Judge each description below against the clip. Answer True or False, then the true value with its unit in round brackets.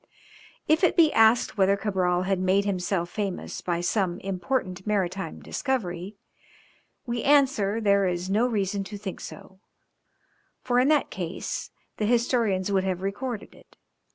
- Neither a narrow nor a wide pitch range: True (3.7 semitones)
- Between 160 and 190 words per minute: False (145 wpm)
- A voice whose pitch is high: True (200 Hz)